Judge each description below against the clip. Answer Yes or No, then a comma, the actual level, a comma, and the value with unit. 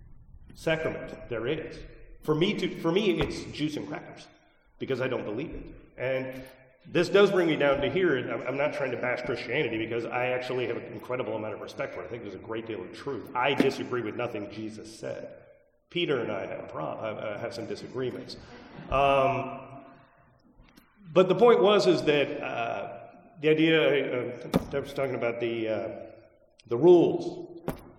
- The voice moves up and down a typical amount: Yes, average, 4.8 semitones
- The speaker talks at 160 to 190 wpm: Yes, average, 180 wpm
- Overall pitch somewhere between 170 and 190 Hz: No, medium, 140 Hz